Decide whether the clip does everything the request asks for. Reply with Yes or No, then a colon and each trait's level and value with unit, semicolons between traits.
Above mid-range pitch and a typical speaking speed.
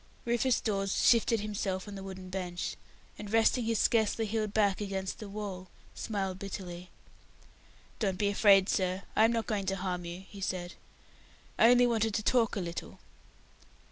Yes: high, 200 Hz; average, 170 wpm